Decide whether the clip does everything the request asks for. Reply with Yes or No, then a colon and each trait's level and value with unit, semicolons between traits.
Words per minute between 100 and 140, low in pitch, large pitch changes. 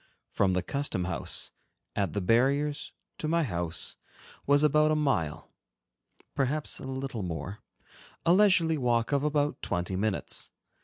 Yes: slow, 135 wpm; low, 130 Hz; wide, 7.7 semitones